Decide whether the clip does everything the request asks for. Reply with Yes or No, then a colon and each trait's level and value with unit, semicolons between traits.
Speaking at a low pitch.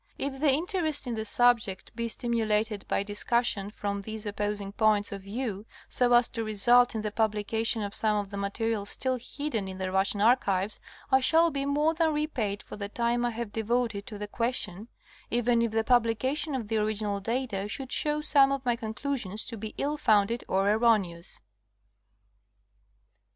No: high, 225 Hz